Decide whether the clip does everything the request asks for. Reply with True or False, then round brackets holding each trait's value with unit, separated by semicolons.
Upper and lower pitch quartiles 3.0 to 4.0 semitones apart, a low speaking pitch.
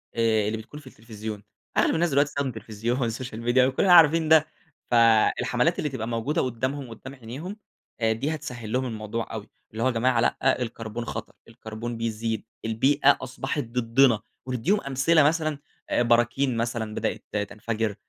True (3.5 semitones; 120 Hz)